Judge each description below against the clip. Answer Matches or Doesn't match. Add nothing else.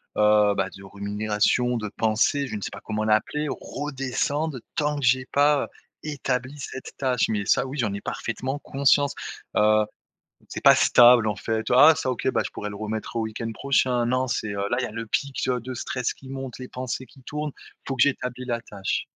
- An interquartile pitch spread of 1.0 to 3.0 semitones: Doesn't match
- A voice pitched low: Matches